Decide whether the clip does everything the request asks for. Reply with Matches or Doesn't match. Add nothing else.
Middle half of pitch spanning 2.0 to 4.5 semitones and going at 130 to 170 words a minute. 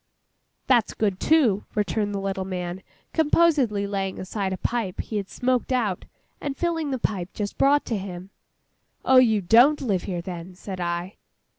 Doesn't match